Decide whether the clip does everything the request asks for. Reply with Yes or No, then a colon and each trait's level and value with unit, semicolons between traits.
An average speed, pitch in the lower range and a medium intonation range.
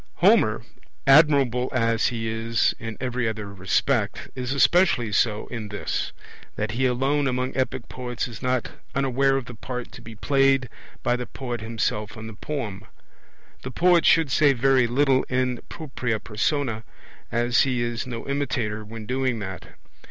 Yes: average, 160 wpm; low, 125 Hz; average, 3.1 semitones